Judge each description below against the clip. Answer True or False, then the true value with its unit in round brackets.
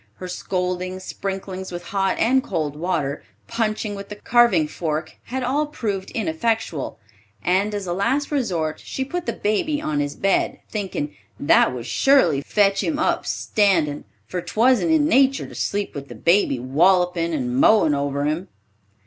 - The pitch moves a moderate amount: False (6.2 semitones)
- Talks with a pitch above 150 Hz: True (190 Hz)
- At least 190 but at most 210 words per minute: False (160 wpm)